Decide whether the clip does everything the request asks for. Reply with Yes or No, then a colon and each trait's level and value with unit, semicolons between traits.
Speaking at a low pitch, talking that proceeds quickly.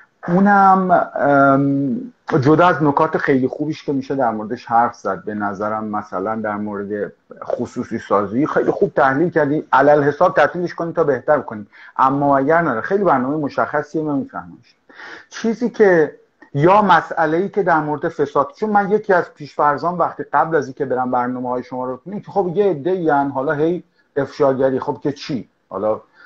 No: medium, 150 Hz; fast, 165 wpm